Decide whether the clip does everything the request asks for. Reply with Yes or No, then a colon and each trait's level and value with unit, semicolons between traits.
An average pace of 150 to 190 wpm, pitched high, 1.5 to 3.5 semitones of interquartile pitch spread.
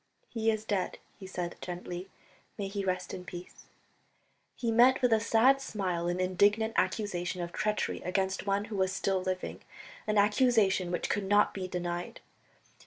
Yes: average, 165 wpm; high, 195 Hz; average, 2.8 semitones